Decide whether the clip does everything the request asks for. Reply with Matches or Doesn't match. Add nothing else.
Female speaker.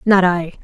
Matches